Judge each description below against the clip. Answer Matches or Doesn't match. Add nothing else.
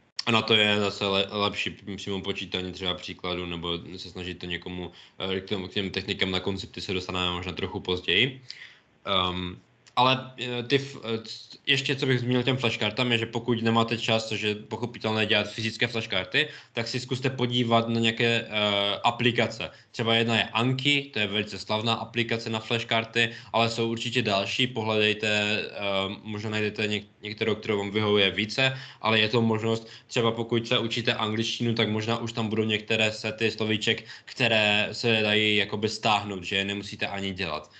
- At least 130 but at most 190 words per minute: Matches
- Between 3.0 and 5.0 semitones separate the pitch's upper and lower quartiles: Doesn't match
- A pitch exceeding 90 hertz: Matches